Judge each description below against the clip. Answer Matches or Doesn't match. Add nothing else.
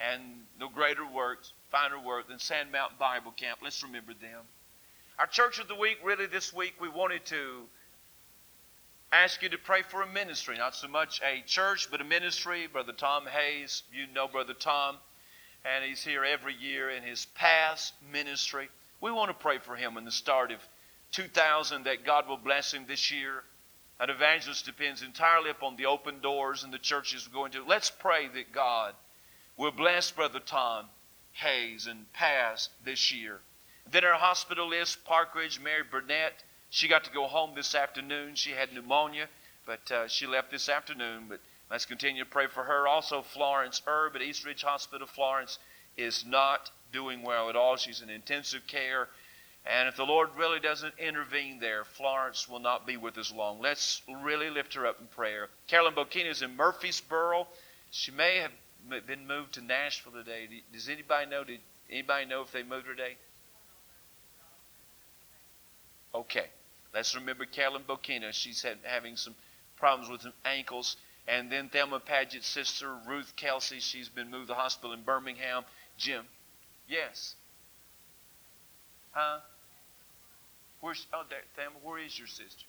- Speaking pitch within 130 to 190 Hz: Matches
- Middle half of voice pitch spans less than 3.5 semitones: Matches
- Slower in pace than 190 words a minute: Matches